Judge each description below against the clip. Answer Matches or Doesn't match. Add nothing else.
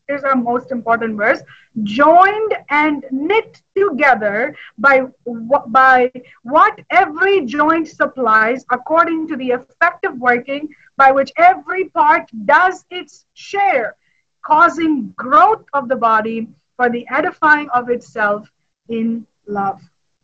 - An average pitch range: Doesn't match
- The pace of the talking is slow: Matches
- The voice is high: Matches